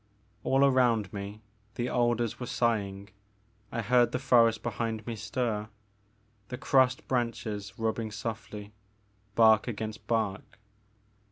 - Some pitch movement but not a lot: No, narrow, 2.2 semitones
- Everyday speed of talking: No, slow, 115 wpm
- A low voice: Yes, low, 115 Hz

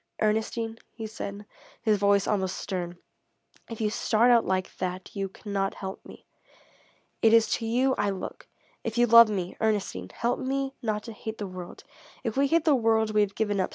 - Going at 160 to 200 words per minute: Yes, average, 190 wpm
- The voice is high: Yes, high, 215 Hz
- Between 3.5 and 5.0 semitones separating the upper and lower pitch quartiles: No, average, 2.7 semitones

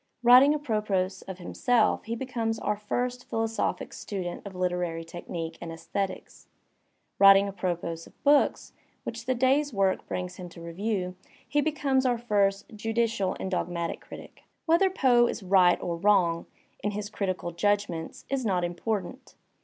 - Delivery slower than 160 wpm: Yes, average, 150 wpm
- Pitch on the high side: Yes, high, 200 Hz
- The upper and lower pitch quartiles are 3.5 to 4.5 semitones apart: No, average, 4.9 semitones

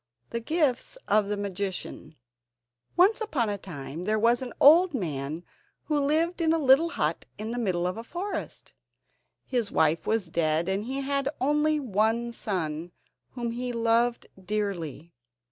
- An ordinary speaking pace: Yes, average, 160 wpm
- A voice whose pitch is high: Yes, high, 230 Hz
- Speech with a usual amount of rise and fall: No, wide, 7.2 semitones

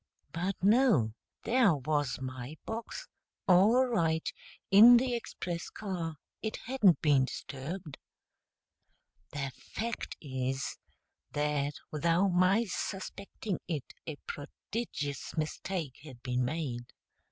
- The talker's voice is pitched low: No, medium, 165 Hz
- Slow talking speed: Yes, slow, 105 wpm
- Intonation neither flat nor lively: No, wide, 6.2 semitones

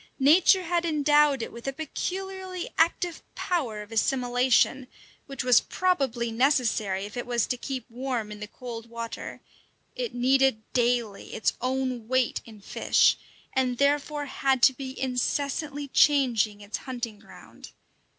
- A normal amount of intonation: Yes, average, 3.7 semitones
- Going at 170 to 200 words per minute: No, average, 140 wpm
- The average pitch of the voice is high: Yes, very high, 260 Hz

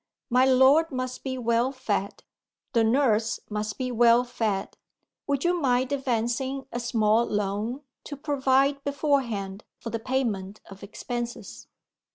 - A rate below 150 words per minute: Yes, slow, 135 wpm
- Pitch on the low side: No, high, 245 Hz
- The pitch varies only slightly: No, average, 3.2 semitones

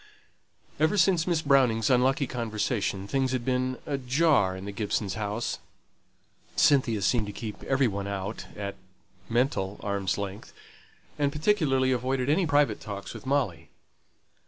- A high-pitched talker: No, low, 125 Hz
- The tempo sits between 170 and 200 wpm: No, slow, 135 wpm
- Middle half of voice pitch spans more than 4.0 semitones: Yes, average, 5.2 semitones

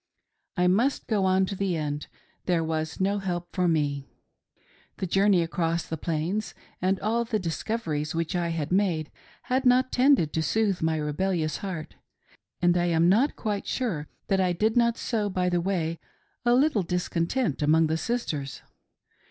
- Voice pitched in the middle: Yes, medium, 180 Hz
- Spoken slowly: No, average, 170 wpm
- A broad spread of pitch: No, average, 4.3 semitones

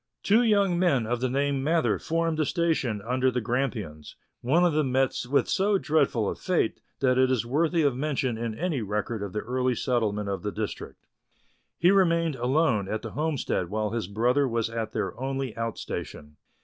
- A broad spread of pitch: Yes, wide, 5.8 semitones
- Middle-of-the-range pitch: No, low, 130 Hz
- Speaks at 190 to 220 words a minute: Yes, average, 195 wpm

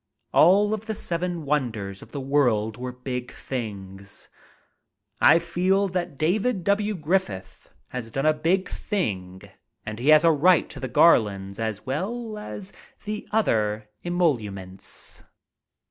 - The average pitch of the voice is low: No, medium, 145 Hz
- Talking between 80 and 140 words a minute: Yes, slow, 135 wpm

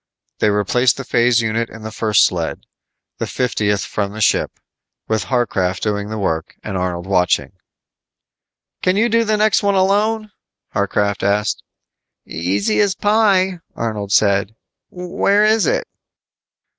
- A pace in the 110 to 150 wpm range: Yes, average, 140 wpm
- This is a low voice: Yes, low, 110 Hz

